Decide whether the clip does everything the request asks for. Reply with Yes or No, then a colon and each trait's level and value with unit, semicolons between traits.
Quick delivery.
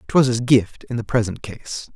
Yes: fast, 215 wpm